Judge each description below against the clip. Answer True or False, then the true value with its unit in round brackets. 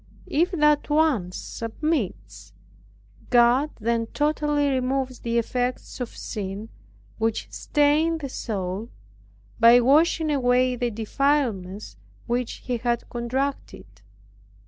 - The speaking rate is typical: False (100 wpm)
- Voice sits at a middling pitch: False (245 Hz)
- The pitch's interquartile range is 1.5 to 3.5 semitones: False (4.4 semitones)